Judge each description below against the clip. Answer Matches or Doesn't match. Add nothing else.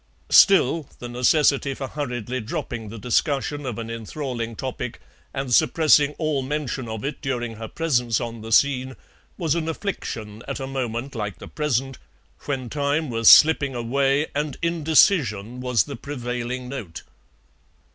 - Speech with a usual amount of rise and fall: Matches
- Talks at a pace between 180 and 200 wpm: Doesn't match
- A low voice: Matches